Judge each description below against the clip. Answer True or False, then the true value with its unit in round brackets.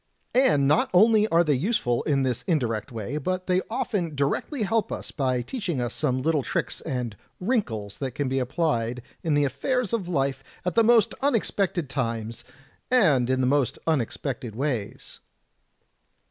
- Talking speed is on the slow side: False (170 wpm)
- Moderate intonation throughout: False (6.6 semitones)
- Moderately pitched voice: True (145 Hz)